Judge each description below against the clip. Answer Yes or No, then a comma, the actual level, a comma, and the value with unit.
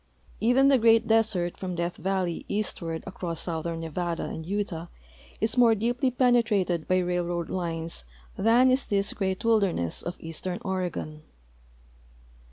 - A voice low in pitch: No, medium, 185 Hz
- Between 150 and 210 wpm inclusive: No, slow, 135 wpm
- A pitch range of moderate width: Yes, average, 4.7 semitones